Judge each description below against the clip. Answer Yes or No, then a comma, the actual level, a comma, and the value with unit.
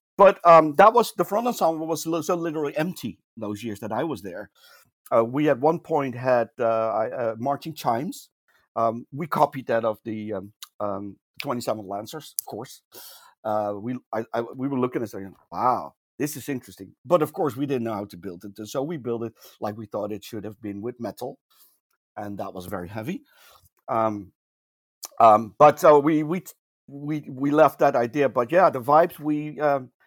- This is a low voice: Yes, low, 125 Hz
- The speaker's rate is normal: Yes, average, 195 wpm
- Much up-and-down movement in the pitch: Yes, wide, 6.0 semitones